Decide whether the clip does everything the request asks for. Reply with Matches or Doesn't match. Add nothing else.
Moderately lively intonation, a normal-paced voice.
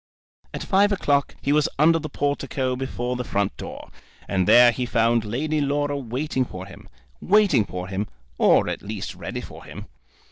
Matches